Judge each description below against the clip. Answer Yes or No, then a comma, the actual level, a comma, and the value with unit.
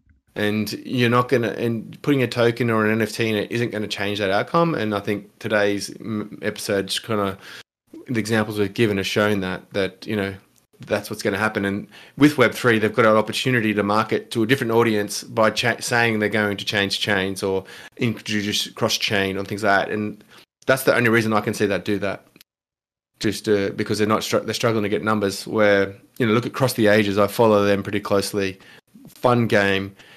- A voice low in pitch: Yes, low, 105 Hz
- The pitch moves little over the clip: Yes, narrow, 2.1 semitones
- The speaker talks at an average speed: No, fast, 210 wpm